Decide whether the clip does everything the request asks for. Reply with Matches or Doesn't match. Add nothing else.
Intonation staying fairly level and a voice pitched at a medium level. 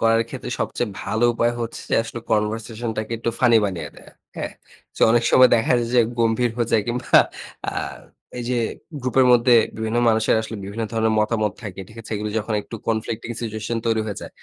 Doesn't match